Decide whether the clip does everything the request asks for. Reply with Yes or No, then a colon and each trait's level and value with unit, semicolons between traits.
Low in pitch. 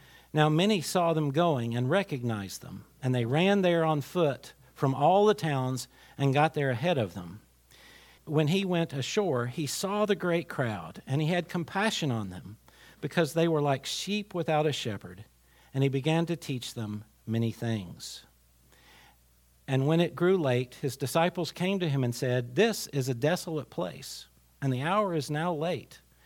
No: medium, 145 Hz